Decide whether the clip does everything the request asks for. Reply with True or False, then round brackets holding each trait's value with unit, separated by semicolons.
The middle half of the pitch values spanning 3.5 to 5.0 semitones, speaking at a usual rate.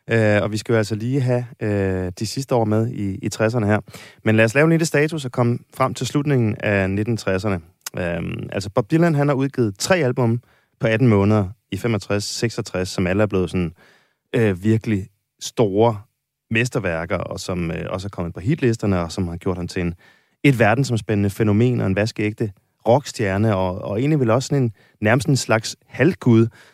True (3.8 semitones; 195 wpm)